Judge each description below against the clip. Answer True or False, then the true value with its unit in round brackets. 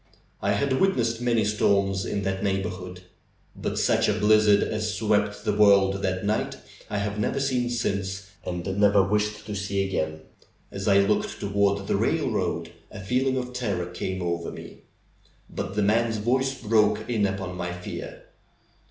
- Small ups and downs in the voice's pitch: True (2.0 semitones)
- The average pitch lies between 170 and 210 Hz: False (100 Hz)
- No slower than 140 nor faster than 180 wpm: True (165 wpm)